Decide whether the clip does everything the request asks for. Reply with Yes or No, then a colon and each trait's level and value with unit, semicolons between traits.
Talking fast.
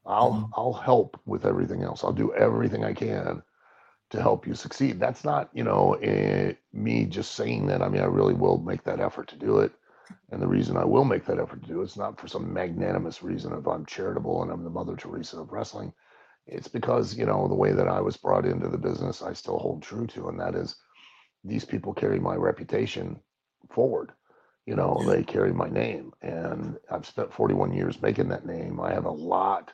Yes: fast, 220 wpm